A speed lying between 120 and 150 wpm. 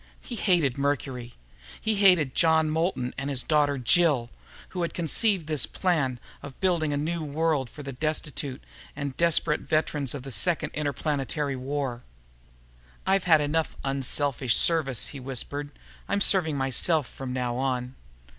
Yes: average, 145 wpm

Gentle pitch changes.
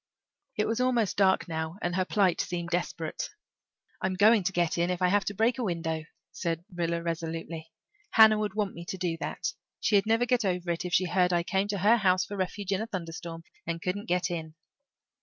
No: average, 3.2 semitones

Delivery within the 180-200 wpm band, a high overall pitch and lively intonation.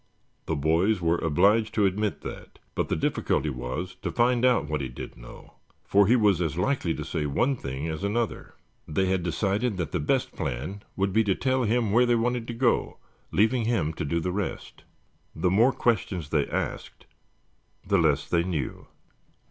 No: average, 190 wpm; very low, 95 Hz; wide, 6.1 semitones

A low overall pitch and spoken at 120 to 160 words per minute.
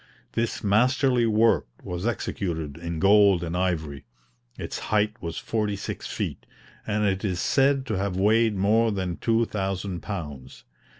Yes: low, 100 Hz; average, 140 wpm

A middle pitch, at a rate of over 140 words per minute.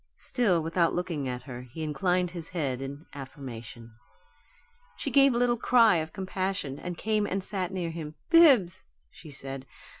Yes: medium, 170 Hz; average, 160 wpm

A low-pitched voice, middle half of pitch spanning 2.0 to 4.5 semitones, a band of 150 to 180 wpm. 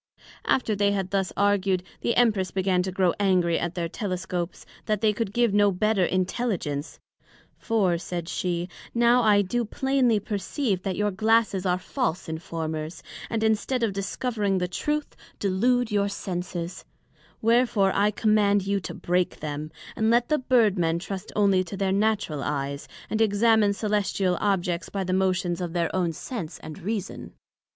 No: high, 195 Hz; average, 3.4 semitones; average, 160 wpm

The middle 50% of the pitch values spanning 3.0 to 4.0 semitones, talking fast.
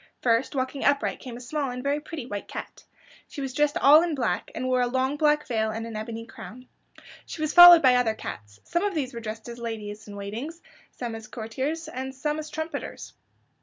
No: average, 4.8 semitones; fast, 215 wpm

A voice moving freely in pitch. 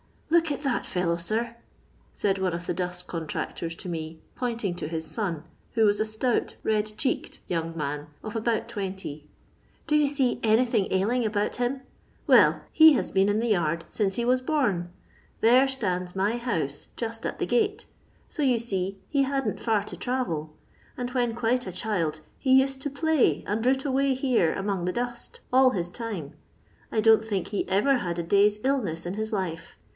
Yes: wide, 5.9 semitones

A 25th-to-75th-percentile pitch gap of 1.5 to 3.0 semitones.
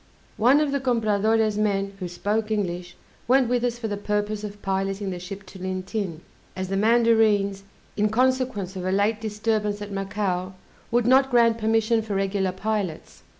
Yes: narrow, 2.5 semitones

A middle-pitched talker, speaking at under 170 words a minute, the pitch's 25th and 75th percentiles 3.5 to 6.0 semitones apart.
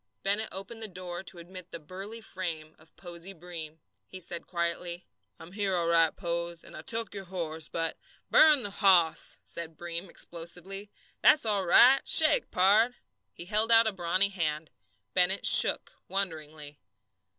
No: medium, 180 Hz; average, 160 wpm; average, 2.9 semitones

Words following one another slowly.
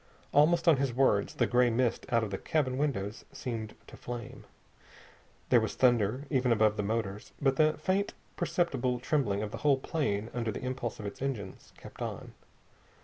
No: average, 175 wpm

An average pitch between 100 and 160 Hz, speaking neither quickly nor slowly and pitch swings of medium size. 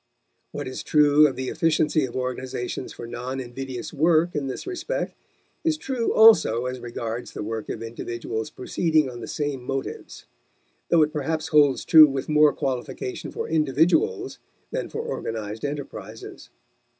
Yes: medium, 140 Hz; average, 150 wpm; average, 4.2 semitones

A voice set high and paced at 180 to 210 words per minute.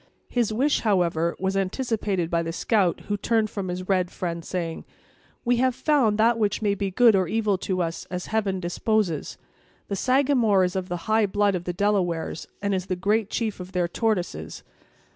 Yes: high, 195 Hz; average, 190 wpm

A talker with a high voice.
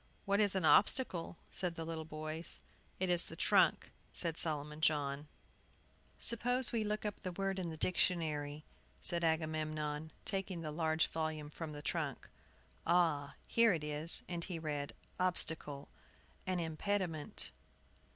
No: medium, 165 Hz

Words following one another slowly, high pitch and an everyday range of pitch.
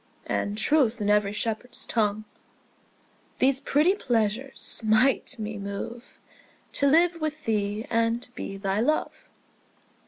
Yes: slow, 120 wpm; high, 230 Hz; average, 4.6 semitones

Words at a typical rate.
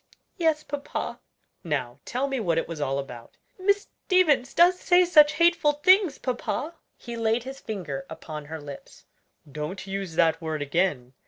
Yes: average, 160 wpm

